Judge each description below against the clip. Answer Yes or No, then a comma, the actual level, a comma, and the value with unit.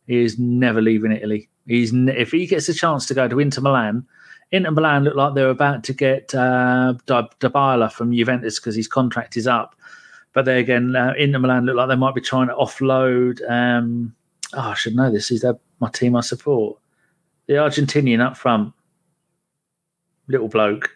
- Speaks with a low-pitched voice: Yes, low, 130 Hz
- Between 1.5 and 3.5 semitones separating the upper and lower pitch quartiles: Yes, average, 2.9 semitones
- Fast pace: No, average, 190 wpm